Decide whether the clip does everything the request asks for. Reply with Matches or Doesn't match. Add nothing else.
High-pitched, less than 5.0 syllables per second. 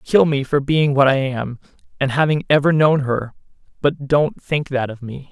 Doesn't match